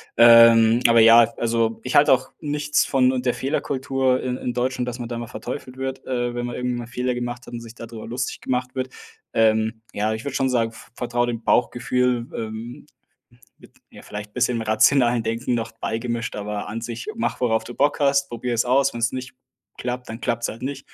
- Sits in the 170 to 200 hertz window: No, low, 120 Hz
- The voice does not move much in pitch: Yes, narrow, 1.8 semitones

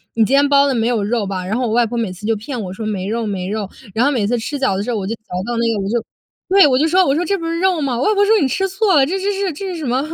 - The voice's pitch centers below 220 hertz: No, high, 245 Hz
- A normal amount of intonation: No, wide, 6.6 semitones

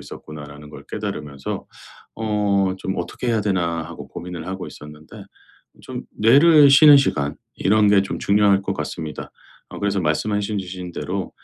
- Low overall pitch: Yes, very low, 95 Hz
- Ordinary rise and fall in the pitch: Yes, average, 4.4 semitones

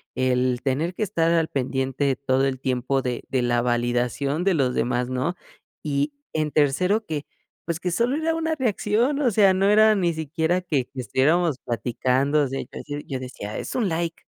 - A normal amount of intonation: No, wide, 5.7 semitones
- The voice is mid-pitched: Yes, medium, 145 Hz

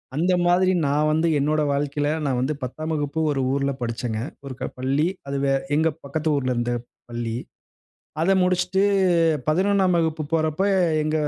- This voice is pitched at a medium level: Yes, medium, 150 Hz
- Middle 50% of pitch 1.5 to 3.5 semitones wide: Yes, average, 3.0 semitones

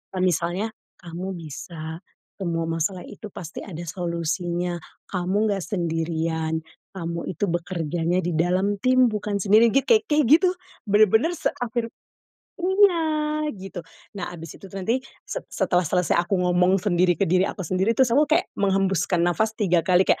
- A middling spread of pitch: Yes, average, 4.0 semitones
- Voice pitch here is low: No, medium, 185 Hz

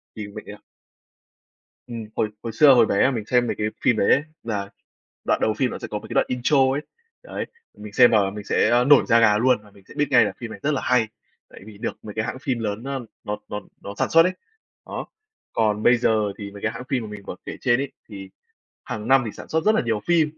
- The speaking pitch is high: No, low, 115 Hz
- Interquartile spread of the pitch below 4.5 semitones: Yes, average, 3.6 semitones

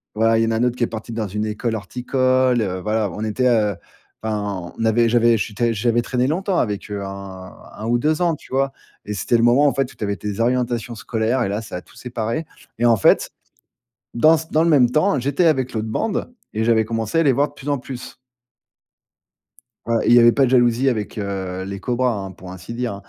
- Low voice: Yes, low, 115 Hz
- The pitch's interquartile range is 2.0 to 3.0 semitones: No, average, 3.4 semitones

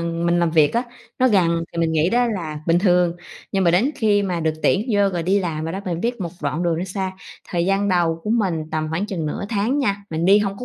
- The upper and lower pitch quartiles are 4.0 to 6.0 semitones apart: No, average, 3.3 semitones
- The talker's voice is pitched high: No, medium, 180 Hz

